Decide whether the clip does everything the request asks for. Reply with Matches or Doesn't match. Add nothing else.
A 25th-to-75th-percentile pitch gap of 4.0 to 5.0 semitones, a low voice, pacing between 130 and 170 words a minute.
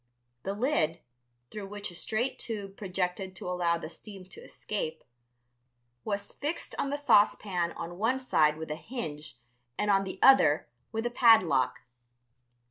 Doesn't match